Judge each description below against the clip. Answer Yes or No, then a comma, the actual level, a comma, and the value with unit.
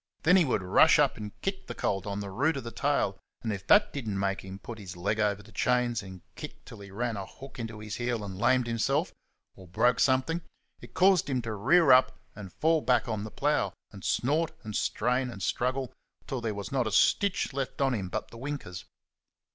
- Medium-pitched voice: No, low, 115 Hz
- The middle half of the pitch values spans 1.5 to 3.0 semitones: No, average, 4.9 semitones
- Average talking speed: No, fast, 225 wpm